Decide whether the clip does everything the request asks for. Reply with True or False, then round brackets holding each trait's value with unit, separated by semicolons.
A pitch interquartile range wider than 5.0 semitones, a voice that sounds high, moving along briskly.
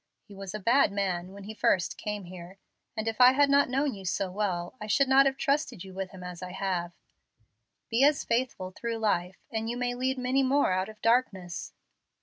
True (5.4 semitones; 210 Hz; 215 wpm)